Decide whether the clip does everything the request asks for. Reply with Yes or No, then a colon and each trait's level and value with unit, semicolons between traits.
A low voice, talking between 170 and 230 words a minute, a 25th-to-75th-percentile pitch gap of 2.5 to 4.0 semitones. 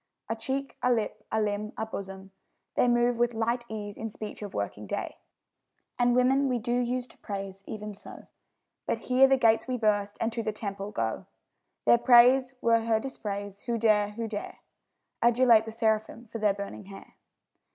No: high, 220 Hz; average, 185 wpm; average, 2.8 semitones